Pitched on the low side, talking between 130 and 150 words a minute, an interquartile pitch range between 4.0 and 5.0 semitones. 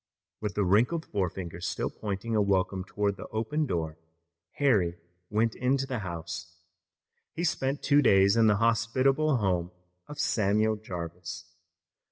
Yes: low, 105 Hz; average, 140 wpm; average, 4.7 semitones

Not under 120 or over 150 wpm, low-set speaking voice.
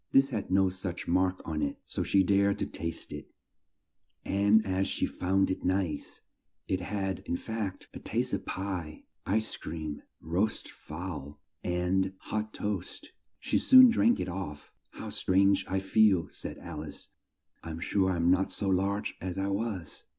No: average, 170 wpm; very low, 95 Hz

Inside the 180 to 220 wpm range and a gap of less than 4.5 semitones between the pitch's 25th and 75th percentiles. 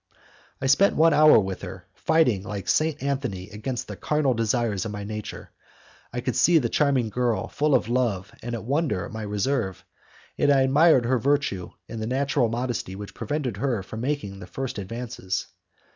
No: average, 185 wpm; average, 4.8 semitones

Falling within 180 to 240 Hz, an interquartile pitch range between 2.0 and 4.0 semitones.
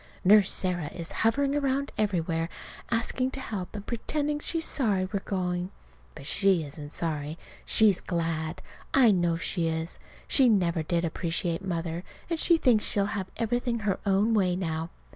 No: high, 190 Hz; average, 5.3 semitones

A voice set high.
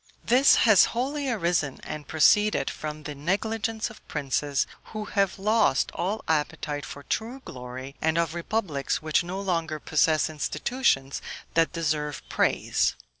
No: medium, 165 Hz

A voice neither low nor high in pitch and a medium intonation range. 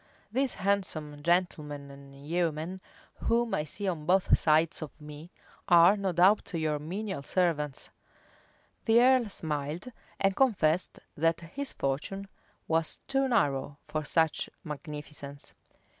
Yes: medium, 165 Hz; average, 4.6 semitones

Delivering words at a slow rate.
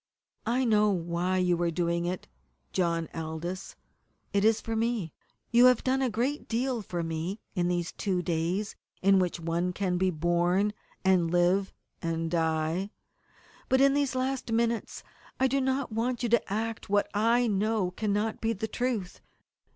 No: average, 165 wpm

